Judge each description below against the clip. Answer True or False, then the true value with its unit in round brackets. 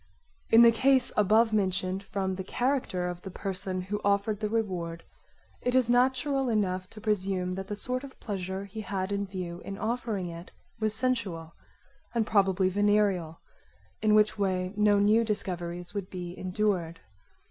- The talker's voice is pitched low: False (200 Hz)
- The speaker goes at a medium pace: True (160 wpm)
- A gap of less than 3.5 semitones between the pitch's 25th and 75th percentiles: True (2.9 semitones)